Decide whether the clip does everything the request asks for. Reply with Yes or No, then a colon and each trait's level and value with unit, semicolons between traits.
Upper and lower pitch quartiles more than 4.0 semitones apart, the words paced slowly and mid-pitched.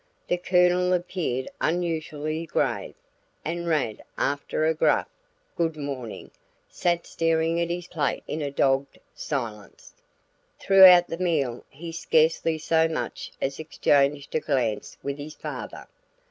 No: average, 3.3 semitones; slow, 130 wpm; medium, 160 Hz